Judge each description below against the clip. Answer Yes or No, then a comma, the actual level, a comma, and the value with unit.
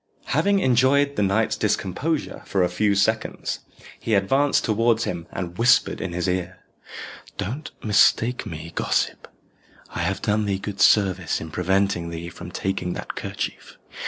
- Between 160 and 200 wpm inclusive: No, average, 150 wpm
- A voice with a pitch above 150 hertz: No, low, 100 Hz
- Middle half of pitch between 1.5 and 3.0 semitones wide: No, average, 4.2 semitones